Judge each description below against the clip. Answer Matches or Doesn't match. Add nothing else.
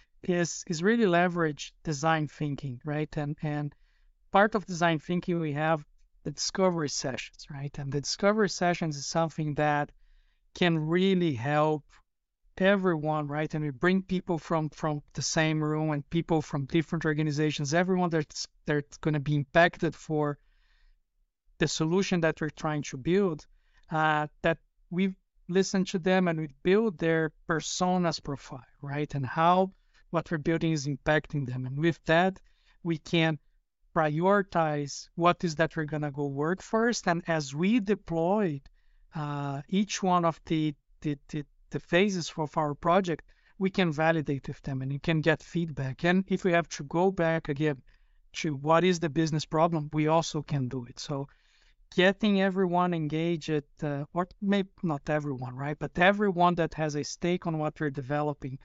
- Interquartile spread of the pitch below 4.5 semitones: Matches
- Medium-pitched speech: Matches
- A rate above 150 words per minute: Matches